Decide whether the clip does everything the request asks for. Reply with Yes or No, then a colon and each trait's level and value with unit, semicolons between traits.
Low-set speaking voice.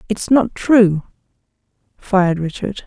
No: high, 200 Hz